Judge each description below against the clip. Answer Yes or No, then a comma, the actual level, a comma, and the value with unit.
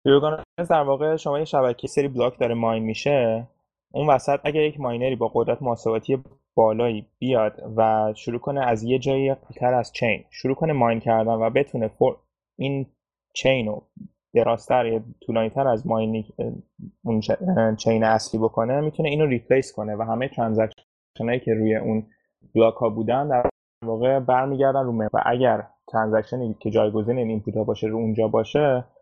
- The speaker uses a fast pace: Yes, fast, 160 wpm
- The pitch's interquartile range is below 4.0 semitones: Yes, average, 3.4 semitones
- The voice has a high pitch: No, low, 120 Hz